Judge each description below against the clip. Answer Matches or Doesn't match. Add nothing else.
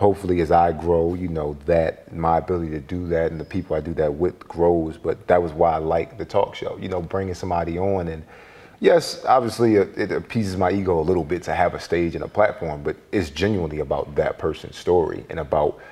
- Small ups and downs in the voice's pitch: Matches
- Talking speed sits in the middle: Doesn't match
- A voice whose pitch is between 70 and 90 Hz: Matches